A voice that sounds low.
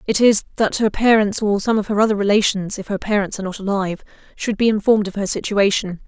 No: high, 205 Hz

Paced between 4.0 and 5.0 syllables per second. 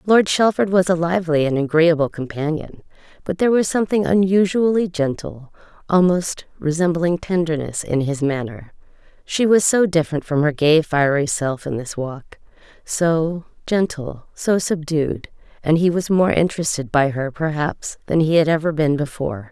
Yes: 4.9 syllables/s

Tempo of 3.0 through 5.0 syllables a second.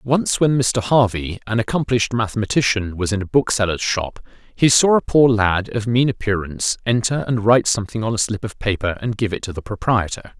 No: 5.6 syllables/s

